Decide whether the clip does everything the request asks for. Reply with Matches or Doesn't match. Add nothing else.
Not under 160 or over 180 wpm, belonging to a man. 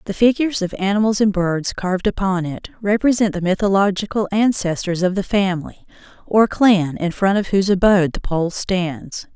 Doesn't match